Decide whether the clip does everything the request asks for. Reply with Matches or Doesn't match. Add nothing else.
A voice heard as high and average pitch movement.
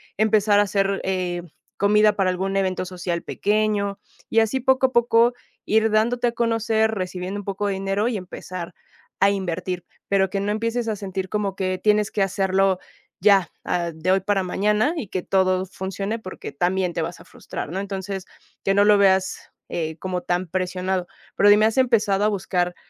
Doesn't match